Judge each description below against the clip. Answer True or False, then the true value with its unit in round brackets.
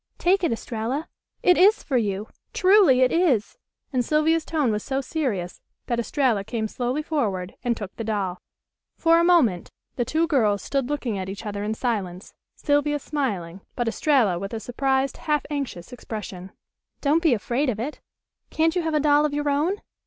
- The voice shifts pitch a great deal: True (6.1 semitones)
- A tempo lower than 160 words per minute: False (185 wpm)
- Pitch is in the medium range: False (255 Hz)